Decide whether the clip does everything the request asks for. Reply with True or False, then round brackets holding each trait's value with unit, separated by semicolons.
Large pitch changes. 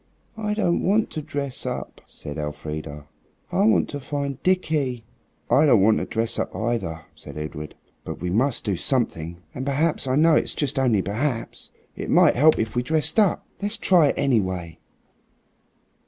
True (8.5 semitones)